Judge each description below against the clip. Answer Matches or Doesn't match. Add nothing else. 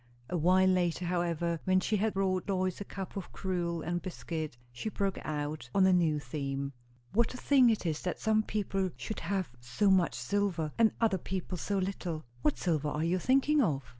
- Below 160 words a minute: Doesn't match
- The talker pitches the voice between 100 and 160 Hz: Doesn't match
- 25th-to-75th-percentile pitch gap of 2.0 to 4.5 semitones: Matches